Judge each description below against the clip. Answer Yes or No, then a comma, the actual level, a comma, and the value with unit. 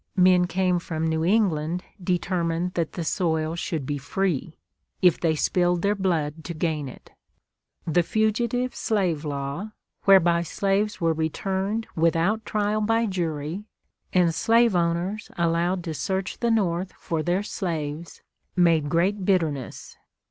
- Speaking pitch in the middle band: Yes, medium, 175 Hz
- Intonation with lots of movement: No, average, 3.2 semitones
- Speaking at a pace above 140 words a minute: No, slow, 135 wpm